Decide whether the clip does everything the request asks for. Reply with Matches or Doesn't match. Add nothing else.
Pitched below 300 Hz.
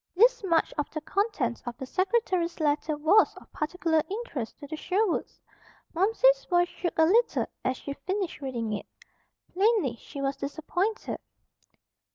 Doesn't match